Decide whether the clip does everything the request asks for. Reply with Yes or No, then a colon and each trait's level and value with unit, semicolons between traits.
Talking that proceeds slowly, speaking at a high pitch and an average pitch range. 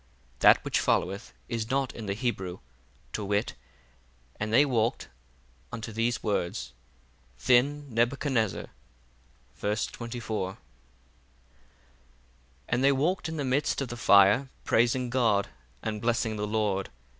No: slow, 120 wpm; low, 110 Hz; average, 4.1 semitones